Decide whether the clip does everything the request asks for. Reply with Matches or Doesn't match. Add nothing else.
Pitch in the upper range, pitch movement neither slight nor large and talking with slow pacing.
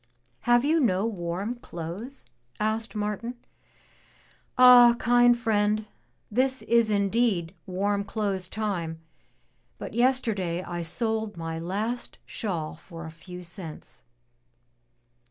Matches